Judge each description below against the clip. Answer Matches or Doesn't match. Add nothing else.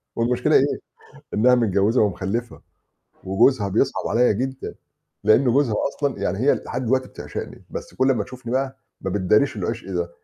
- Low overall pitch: Matches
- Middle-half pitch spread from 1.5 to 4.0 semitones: Doesn't match